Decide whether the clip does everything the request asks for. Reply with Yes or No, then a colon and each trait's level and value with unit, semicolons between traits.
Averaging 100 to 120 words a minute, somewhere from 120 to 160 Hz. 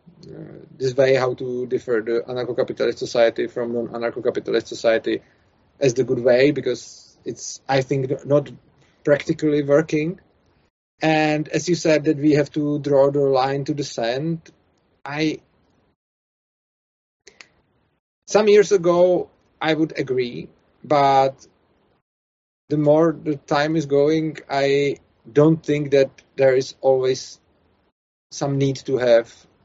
No: average, 130 wpm; medium, 140 Hz